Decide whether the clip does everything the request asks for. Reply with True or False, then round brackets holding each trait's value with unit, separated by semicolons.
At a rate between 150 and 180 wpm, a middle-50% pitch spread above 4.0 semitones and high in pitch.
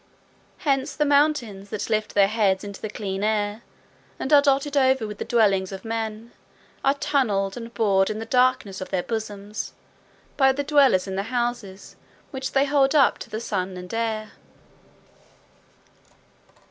True (160 wpm; 5.0 semitones; 220 Hz)